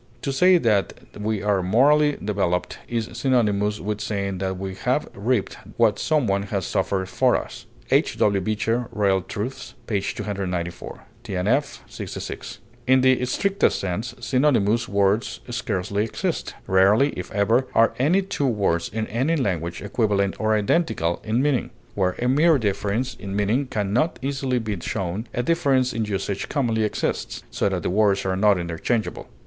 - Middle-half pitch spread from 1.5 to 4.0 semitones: No, average, 4.5 semitones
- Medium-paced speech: Yes, average, 160 wpm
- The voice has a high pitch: No, low, 105 Hz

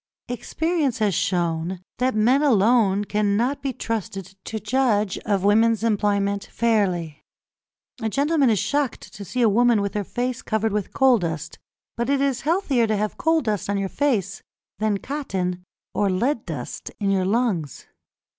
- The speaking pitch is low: No, high, 215 Hz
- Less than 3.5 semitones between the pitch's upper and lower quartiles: No, average, 4.2 semitones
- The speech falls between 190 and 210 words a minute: No, average, 160 wpm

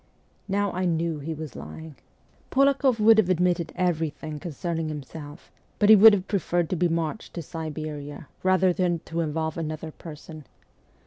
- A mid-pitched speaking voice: Yes, medium, 165 Hz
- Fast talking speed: No, average, 155 wpm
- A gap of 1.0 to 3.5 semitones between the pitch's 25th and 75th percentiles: Yes, average, 2.9 semitones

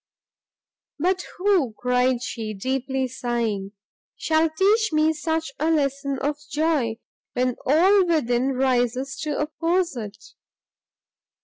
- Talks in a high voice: Yes, very high, 275 Hz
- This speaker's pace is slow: Yes, slow, 110 wpm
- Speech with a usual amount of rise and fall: Yes, average, 4.4 semitones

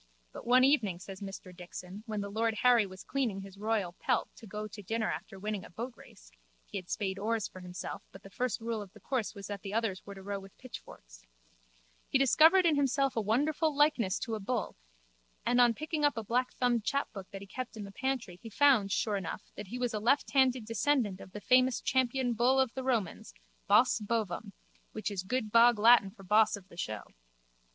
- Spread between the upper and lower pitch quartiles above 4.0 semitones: Yes, average, 4.4 semitones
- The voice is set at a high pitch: Yes, high, 220 Hz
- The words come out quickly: Yes, fast, 210 wpm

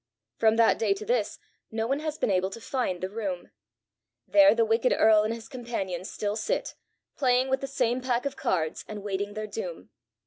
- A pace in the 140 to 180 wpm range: No, average, 200 wpm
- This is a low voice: No, high, 225 Hz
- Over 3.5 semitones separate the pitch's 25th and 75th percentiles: Yes, average, 4.0 semitones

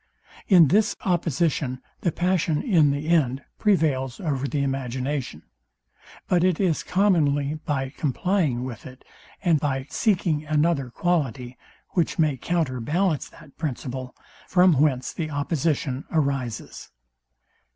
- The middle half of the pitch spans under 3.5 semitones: No, average, 4.4 semitones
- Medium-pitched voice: Yes, medium, 150 Hz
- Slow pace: Yes, slow, 120 wpm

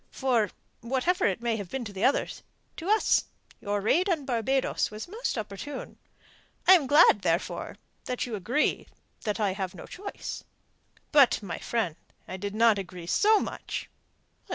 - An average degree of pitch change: No, wide, 6.2 semitones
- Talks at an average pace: Yes, average, 155 wpm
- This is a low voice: No, high, 230 Hz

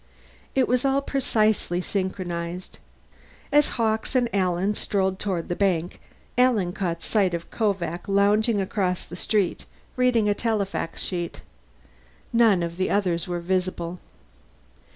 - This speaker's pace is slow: Yes, slow, 130 wpm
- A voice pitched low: No, high, 195 Hz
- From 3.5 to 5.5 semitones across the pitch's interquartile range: Yes, average, 3.8 semitones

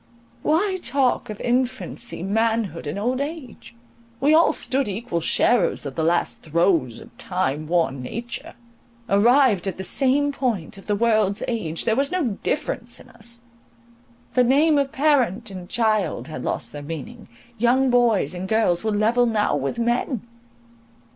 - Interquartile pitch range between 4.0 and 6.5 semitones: Yes, average, 5.3 semitones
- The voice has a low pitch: No, high, 230 Hz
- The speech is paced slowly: No, average, 155 wpm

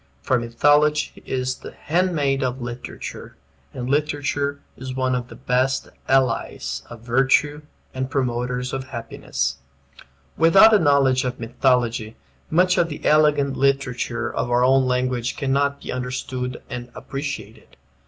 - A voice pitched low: Yes, low, 130 Hz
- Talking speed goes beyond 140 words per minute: No, slow, 135 wpm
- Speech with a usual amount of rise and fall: No, narrow, 2.3 semitones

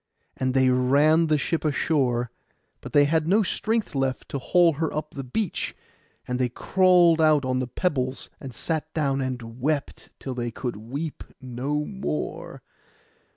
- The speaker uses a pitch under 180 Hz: Yes, medium, 140 Hz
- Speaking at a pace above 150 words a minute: Yes, average, 160 wpm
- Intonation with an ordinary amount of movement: Yes, average, 3.9 semitones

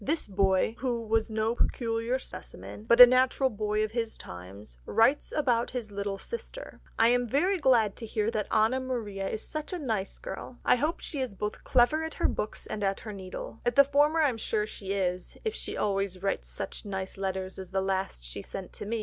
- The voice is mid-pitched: No, high, 220 Hz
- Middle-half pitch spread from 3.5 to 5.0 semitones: Yes, average, 4.5 semitones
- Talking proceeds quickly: Yes, fast, 215 wpm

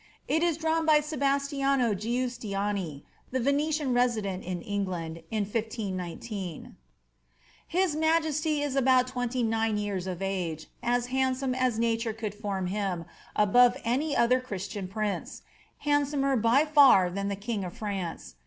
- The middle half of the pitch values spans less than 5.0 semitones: No, wide, 5.6 semitones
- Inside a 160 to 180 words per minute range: No, average, 140 wpm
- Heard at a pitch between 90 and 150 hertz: No, high, 230 Hz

